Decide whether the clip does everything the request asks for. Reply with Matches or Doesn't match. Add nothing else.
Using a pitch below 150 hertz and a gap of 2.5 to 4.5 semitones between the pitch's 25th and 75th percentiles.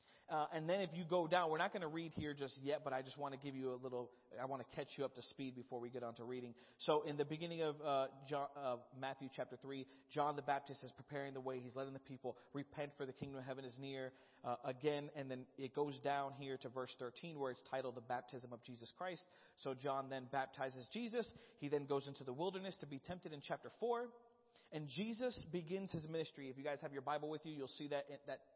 Matches